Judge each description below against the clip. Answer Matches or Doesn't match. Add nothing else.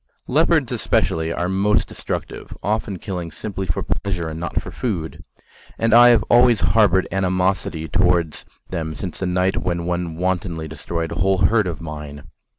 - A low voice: Matches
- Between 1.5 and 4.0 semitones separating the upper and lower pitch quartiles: Matches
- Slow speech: Doesn't match